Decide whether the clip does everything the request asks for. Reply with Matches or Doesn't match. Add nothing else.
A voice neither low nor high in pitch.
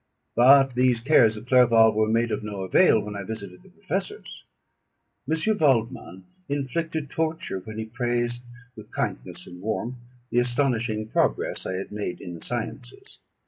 Doesn't match